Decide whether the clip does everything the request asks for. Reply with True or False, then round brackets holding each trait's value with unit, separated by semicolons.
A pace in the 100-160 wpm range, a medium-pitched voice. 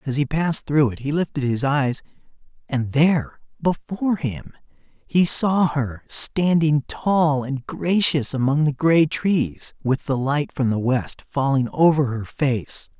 True (155 wpm; 145 Hz)